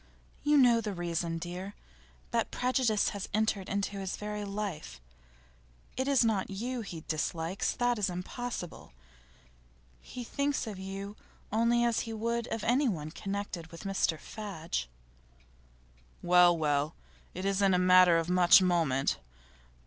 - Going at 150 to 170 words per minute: No, slow, 135 wpm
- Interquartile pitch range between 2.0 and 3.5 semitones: No, average, 4.5 semitones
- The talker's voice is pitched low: No, high, 195 Hz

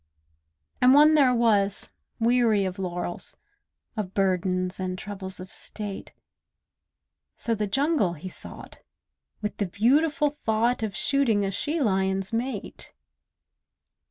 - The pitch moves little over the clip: No, average, 4.7 semitones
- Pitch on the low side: No, high, 210 Hz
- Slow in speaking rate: Yes, slow, 120 wpm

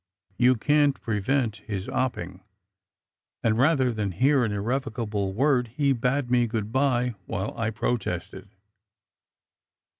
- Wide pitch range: No, average, 4.2 semitones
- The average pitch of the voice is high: No, low, 120 Hz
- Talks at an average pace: No, slow, 125 wpm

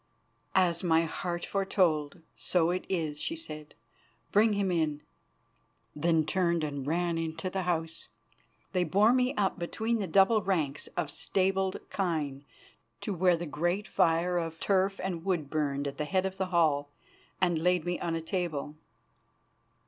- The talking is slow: No, average, 155 wpm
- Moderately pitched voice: Yes, medium, 175 Hz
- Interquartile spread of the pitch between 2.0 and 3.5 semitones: Yes, average, 3.1 semitones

